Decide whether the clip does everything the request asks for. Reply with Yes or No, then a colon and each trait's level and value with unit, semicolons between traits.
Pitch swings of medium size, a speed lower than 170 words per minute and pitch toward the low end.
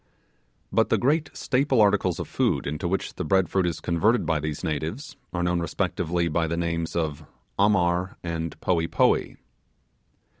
Yes: average, 3.0 semitones; average, 160 wpm; very low, 85 Hz